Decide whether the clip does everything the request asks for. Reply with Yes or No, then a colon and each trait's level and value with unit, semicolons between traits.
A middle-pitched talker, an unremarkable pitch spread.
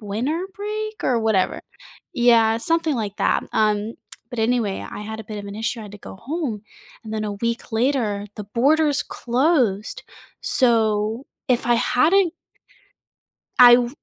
No: high, 230 Hz; average, 4.1 semitones